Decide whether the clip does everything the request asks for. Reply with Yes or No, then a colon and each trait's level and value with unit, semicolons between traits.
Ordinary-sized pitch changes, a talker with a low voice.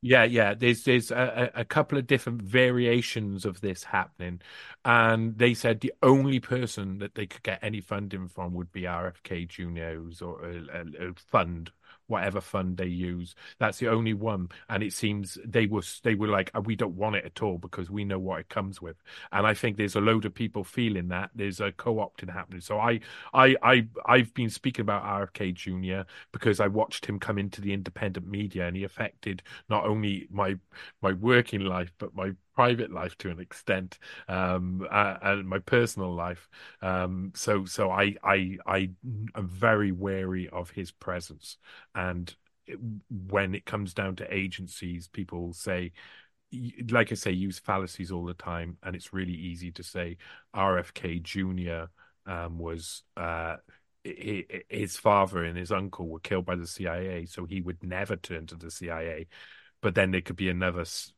Yes: average, 3.2 semitones; very low, 95 Hz